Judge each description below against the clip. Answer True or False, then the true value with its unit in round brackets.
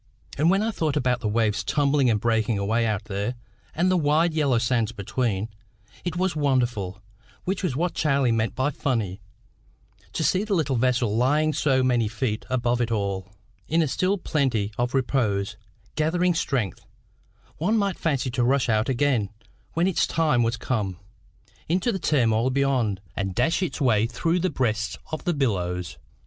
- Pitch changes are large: True (5.8 semitones)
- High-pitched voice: False (130 Hz)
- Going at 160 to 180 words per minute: True (170 wpm)